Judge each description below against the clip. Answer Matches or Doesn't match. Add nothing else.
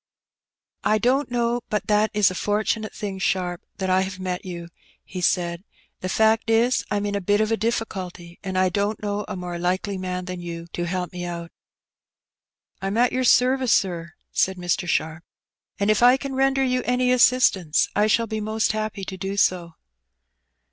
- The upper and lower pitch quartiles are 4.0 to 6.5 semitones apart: Doesn't match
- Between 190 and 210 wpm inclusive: Matches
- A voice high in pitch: Matches